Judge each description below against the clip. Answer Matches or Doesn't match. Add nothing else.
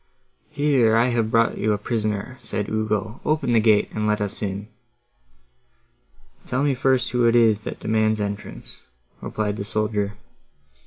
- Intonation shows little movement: Matches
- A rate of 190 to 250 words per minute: Doesn't match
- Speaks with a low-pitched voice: Matches